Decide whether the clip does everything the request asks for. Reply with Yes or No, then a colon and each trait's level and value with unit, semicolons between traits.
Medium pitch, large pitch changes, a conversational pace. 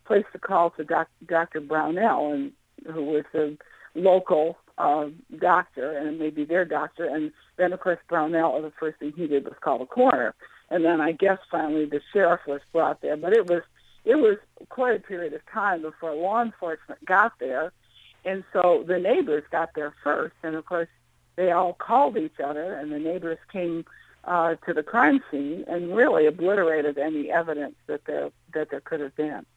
No: medium, 165 Hz; average, 2.8 semitones; average, 190 wpm